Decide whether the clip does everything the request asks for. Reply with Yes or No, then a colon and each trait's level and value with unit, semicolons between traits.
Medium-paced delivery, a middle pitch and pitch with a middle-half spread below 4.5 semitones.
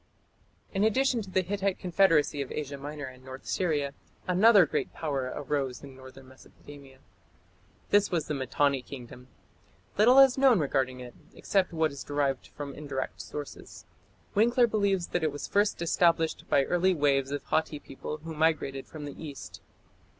No: average, 165 wpm; medium, 150 Hz; wide, 5.4 semitones